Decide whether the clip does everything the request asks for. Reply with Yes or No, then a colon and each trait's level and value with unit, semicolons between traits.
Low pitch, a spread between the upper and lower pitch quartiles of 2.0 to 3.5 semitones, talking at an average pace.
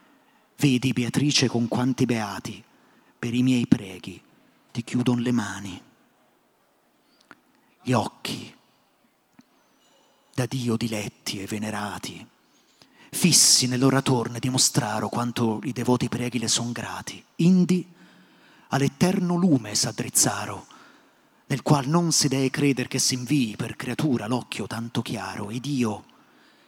No: low, 125 Hz; average, 3.2 semitones; slow, 110 wpm